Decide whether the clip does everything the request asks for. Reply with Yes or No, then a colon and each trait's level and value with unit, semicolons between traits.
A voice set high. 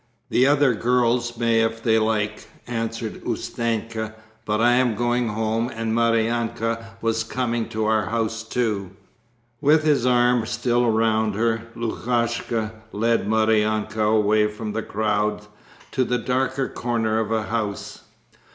No: low, 115 Hz